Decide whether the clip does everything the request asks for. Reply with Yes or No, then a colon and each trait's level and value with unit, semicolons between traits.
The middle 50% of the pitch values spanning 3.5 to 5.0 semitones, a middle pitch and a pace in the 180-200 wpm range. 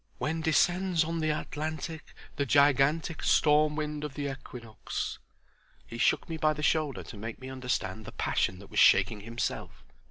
No: average, 3.9 semitones; medium, 150 Hz; average, 165 wpm